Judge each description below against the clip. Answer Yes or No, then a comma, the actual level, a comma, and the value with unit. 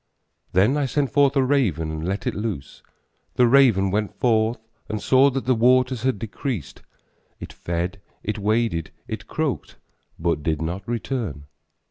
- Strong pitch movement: Yes, wide, 6.1 semitones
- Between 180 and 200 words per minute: No, average, 155 wpm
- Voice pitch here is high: No, low, 110 Hz